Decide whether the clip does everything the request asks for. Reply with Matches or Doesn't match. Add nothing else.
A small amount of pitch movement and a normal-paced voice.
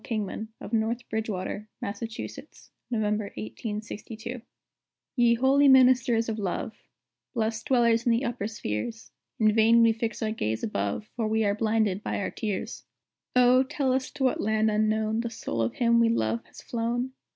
Matches